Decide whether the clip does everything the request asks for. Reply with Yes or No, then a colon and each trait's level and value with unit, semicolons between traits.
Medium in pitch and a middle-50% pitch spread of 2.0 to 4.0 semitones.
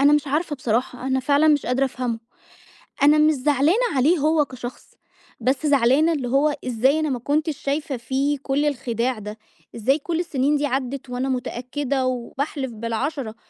No: very high, 270 Hz; average, 2.9 semitones